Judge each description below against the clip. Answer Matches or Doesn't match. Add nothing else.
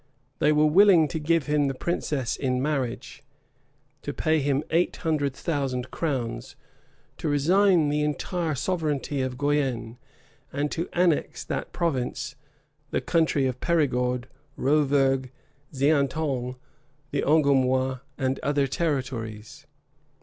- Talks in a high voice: Doesn't match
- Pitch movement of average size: Matches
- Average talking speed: Doesn't match